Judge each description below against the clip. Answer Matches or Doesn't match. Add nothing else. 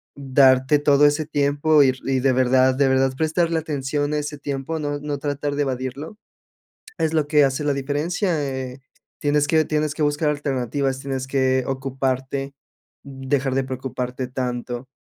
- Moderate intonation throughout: Doesn't match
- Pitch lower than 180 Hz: Matches